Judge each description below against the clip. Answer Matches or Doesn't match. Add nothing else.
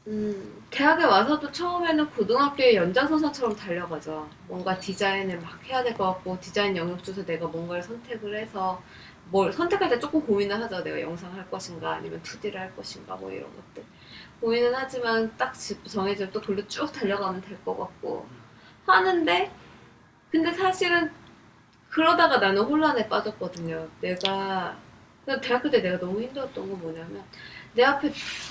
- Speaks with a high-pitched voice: Matches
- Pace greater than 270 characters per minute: Matches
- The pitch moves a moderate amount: Doesn't match